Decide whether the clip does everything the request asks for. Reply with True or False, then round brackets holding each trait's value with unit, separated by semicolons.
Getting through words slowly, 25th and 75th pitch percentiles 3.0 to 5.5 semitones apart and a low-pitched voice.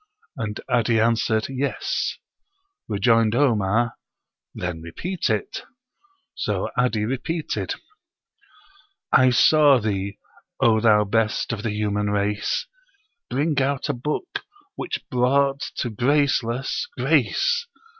True (105 wpm; 4.4 semitones; 120 Hz)